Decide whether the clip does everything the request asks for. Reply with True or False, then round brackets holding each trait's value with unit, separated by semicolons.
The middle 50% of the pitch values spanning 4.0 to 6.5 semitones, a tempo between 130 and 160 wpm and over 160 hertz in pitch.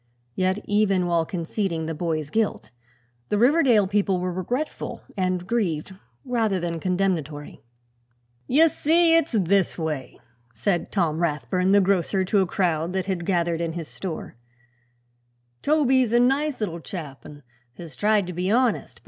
True (4.3 semitones; 150 wpm; 185 Hz)